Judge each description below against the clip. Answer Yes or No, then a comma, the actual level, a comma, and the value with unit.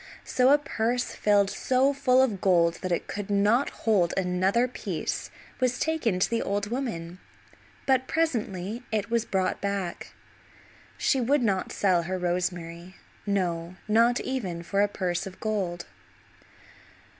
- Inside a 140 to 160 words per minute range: Yes, average, 145 wpm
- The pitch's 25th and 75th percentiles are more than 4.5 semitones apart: Yes, average, 5.1 semitones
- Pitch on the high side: Yes, high, 200 Hz